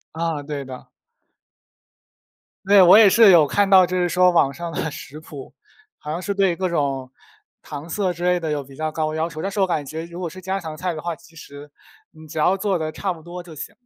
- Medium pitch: Yes, medium, 170 Hz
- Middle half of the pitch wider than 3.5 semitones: No, average, 3.0 semitones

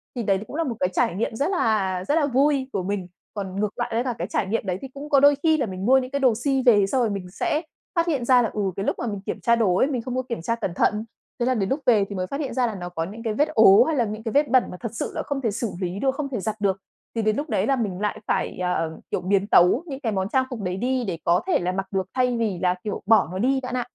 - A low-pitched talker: No, high, 225 Hz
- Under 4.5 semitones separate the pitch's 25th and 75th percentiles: No, average, 5.2 semitones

